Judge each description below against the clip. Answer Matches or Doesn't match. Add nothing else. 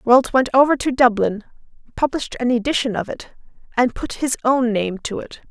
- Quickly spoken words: Doesn't match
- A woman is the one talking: Matches